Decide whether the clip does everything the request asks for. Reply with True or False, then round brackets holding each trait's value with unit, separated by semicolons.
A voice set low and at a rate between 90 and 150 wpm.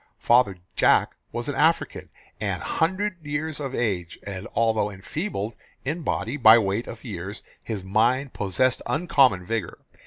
True (115 Hz; 145 wpm)